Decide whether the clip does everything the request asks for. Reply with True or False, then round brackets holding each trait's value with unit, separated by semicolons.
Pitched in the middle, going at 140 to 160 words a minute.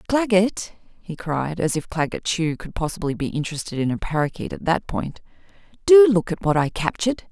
False (180 Hz; 190 wpm)